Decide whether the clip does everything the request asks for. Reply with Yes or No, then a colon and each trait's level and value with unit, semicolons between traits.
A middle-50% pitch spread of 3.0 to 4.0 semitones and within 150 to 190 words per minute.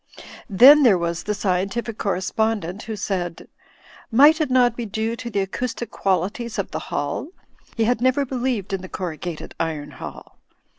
No: average, 4.7 semitones; average, 165 wpm